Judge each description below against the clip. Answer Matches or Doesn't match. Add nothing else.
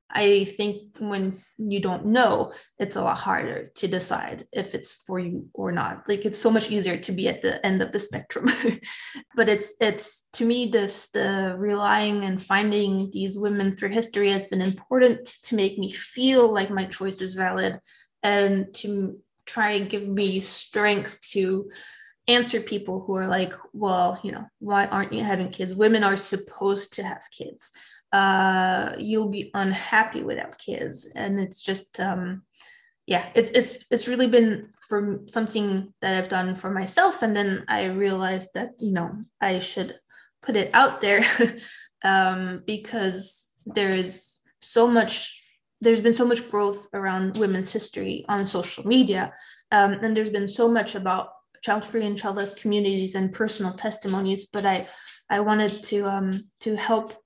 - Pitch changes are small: Matches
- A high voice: Matches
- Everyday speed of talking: Matches